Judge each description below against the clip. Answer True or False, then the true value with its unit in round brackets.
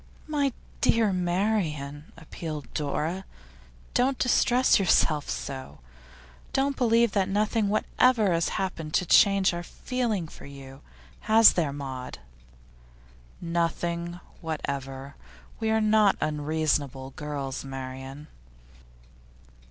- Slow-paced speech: True (100 wpm)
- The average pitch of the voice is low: False (170 Hz)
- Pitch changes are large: True (7.1 semitones)